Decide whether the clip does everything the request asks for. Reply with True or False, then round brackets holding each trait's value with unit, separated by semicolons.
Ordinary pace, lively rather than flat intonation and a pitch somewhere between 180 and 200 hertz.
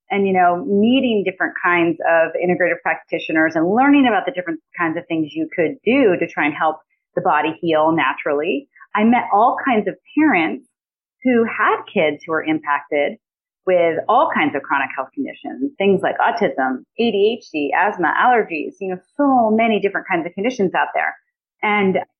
True (175 wpm; 5.7 semitones; 185 Hz)